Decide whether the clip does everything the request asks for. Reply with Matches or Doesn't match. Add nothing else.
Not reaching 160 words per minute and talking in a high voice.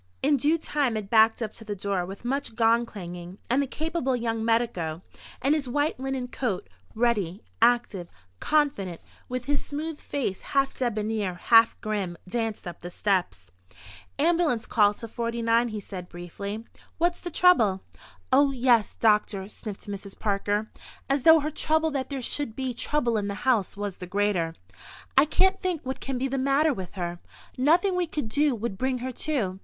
Doesn't match